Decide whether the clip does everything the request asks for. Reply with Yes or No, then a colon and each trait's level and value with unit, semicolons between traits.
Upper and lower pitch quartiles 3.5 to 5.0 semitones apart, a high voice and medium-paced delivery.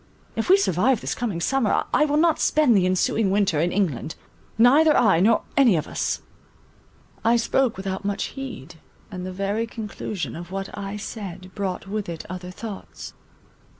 Yes: average, 4.2 semitones; high, 200 Hz; average, 170 wpm